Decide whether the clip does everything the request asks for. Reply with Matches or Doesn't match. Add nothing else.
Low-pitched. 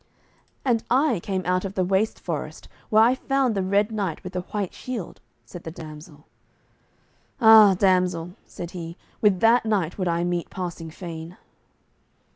Doesn't match